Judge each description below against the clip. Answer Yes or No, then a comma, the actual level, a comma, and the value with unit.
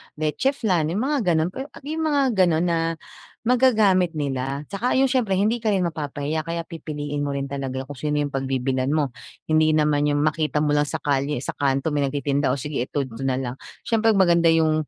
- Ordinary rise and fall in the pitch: Yes, average, 4.8 semitones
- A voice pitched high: No, medium, 155 Hz